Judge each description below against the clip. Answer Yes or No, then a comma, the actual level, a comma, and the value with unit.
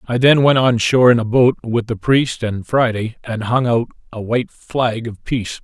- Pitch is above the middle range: No, low, 120 Hz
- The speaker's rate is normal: No, fast, 225 wpm